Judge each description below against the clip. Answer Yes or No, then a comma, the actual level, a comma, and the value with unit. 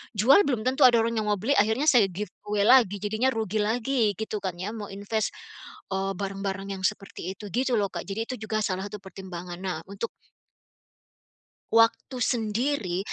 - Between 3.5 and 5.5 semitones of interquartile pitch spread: No, average, 2.9 semitones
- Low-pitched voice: No, high, 210 Hz